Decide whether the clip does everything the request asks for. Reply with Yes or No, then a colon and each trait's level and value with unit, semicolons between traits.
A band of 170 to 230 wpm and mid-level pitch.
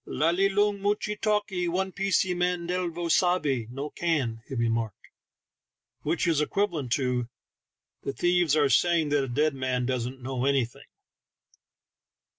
No: average, 140 wpm; medium, 155 Hz